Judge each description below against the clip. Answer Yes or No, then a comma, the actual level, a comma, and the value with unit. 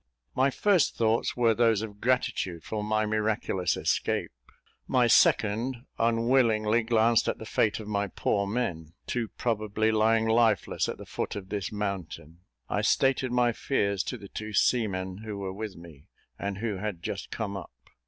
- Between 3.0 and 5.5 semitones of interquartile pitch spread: No, narrow, 2.6 semitones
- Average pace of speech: Yes, average, 165 wpm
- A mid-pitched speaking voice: No, low, 110 Hz